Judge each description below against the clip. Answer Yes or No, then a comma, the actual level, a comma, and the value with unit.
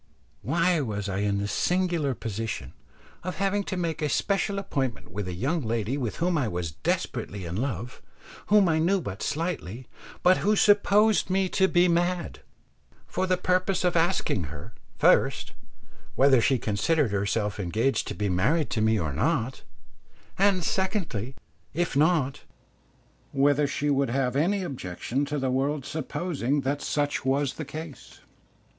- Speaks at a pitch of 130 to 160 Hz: Yes, medium, 140 Hz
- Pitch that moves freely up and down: Yes, wide, 7.8 semitones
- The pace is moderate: Yes, average, 155 wpm